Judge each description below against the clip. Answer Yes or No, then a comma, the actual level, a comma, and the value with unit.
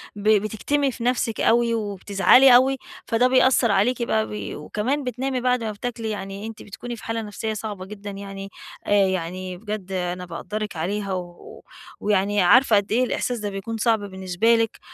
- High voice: Yes, high, 215 Hz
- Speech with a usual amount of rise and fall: Yes, average, 3.2 semitones